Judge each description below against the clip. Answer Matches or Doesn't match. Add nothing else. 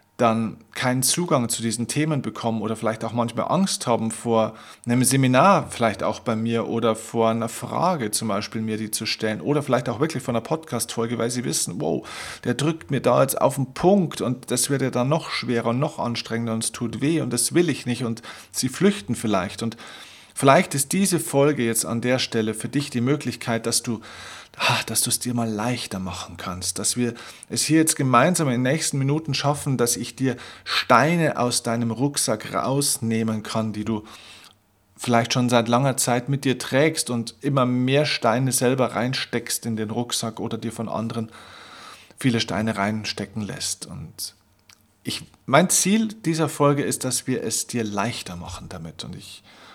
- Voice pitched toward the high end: Doesn't match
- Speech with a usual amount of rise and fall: Matches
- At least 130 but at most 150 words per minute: Doesn't match